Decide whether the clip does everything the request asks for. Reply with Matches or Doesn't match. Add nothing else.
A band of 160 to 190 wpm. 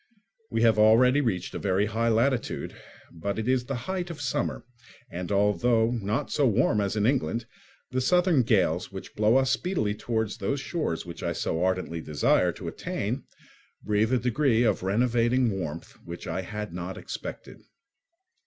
Matches